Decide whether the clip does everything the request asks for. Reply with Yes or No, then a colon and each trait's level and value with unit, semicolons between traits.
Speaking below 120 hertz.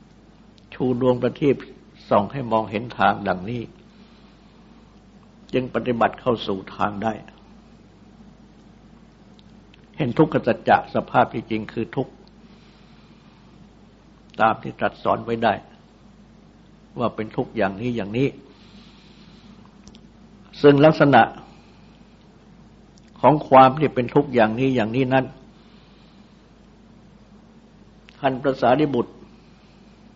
No: low, 125 Hz